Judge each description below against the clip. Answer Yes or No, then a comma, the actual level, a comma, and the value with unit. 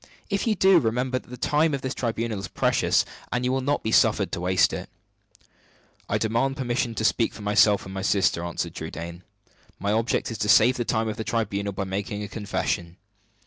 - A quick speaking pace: Yes, fast, 220 wpm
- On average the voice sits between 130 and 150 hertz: No, low, 110 Hz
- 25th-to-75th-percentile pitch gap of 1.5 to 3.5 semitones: No, average, 4.2 semitones